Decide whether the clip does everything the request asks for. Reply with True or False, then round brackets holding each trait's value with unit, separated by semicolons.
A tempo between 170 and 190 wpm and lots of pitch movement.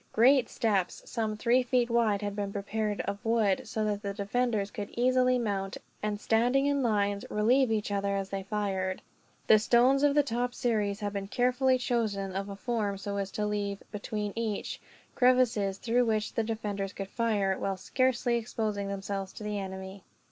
False (180 wpm; 3.1 semitones)